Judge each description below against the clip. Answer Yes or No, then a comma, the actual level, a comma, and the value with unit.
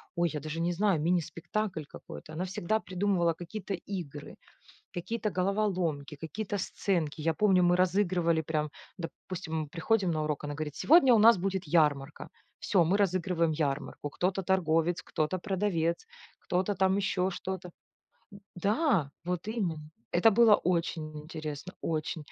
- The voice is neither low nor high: Yes, medium, 175 Hz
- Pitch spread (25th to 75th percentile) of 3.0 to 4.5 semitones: Yes, average, 3.6 semitones